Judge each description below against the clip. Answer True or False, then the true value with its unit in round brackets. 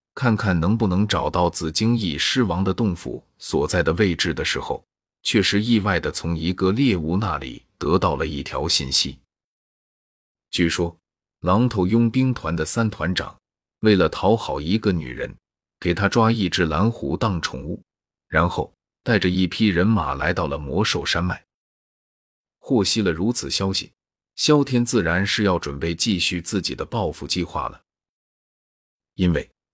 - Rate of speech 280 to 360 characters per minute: False (230 characters per minute)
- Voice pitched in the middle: False (95 Hz)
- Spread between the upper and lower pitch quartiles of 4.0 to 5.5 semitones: True (4.4 semitones)